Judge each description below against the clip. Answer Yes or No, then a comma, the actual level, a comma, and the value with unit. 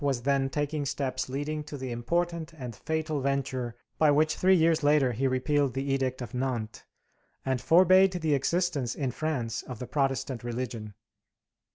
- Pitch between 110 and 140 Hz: Yes, low, 135 Hz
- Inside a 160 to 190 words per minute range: Yes, average, 165 wpm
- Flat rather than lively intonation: No, average, 3.4 semitones